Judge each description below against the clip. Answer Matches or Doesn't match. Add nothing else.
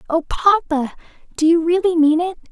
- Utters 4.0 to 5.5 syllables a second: Matches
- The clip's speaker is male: Doesn't match